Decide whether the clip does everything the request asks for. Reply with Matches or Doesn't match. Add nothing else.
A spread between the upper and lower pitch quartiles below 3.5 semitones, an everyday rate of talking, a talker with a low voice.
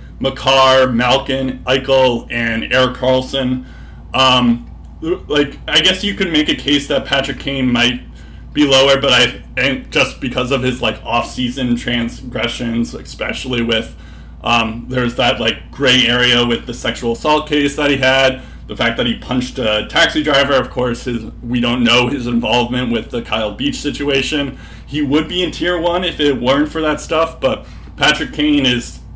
Matches